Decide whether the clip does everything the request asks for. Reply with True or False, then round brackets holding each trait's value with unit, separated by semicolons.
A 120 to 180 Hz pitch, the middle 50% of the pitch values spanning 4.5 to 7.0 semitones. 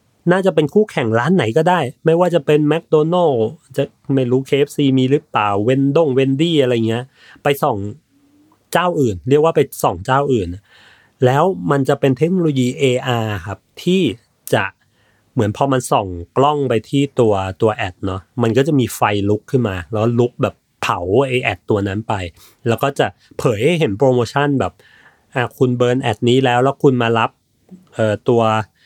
True (130 Hz; 4.8 semitones)